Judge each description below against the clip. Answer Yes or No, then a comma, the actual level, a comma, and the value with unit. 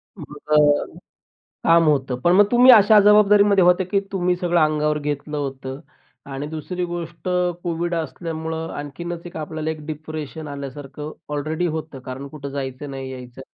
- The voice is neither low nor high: Yes, medium, 155 Hz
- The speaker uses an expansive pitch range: No, average, 3.3 semitones